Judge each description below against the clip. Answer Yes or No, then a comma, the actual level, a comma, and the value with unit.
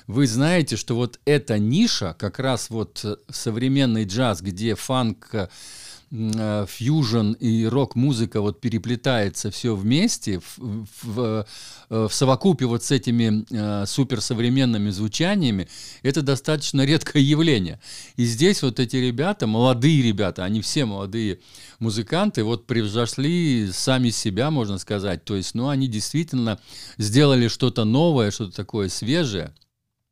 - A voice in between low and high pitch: No, low, 120 Hz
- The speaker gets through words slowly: No, average, 120 wpm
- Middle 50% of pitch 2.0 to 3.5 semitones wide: No, average, 3.9 semitones